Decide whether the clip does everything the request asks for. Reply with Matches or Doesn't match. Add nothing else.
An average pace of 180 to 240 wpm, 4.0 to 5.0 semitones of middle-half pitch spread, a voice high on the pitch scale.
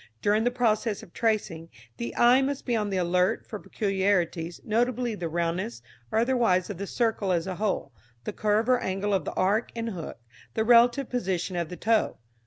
Matches